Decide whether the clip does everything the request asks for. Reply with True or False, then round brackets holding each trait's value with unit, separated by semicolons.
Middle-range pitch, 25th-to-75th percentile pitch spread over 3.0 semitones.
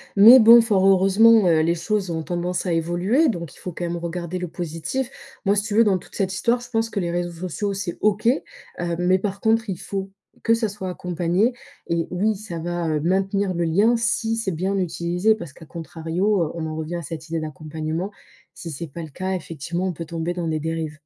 True (180 Hz; 3.6 semitones)